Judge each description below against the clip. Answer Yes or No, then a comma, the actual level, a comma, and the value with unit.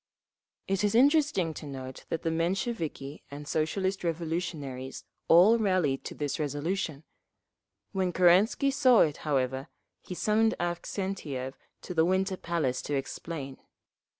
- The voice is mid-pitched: Yes, medium, 170 Hz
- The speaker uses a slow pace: Yes, slow, 125 wpm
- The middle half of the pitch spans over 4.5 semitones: Yes, average, 5.0 semitones